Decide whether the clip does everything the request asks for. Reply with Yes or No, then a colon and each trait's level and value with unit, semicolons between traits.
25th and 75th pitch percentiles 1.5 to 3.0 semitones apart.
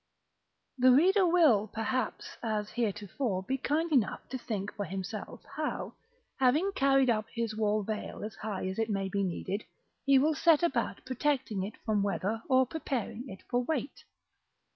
No: average, 4.7 semitones